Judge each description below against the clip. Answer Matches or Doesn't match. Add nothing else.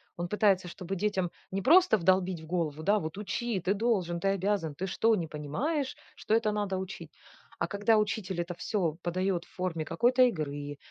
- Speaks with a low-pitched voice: Doesn't match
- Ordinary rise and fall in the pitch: Matches